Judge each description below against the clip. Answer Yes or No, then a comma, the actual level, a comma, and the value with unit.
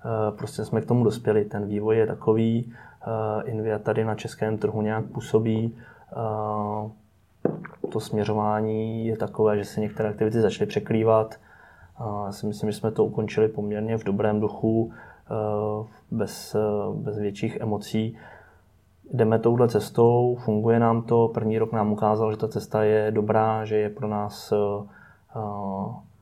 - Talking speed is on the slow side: No, average, 135 wpm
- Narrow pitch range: Yes, narrow, 1.0 semitones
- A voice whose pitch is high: No, low, 110 Hz